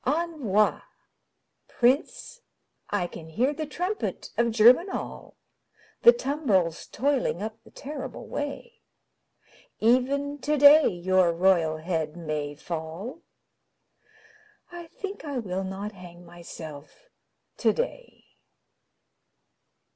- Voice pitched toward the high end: Yes, high, 225 Hz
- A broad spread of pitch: Yes, wide, 8.9 semitones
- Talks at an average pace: No, slow, 95 wpm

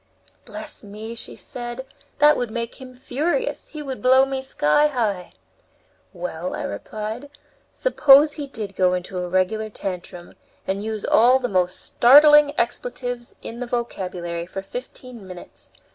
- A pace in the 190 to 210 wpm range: No, average, 145 wpm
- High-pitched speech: Yes, high, 235 Hz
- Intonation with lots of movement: Yes, wide, 5.7 semitones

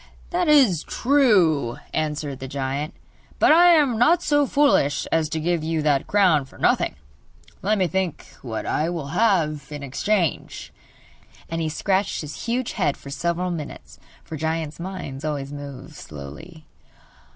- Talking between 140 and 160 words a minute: Yes, average, 150 wpm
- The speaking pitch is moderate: Yes, medium, 160 Hz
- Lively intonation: Yes, wide, 5.7 semitones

